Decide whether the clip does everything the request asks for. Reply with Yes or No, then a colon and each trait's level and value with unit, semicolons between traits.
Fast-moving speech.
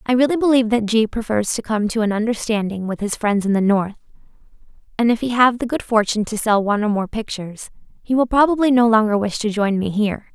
Yes: fast, 230 wpm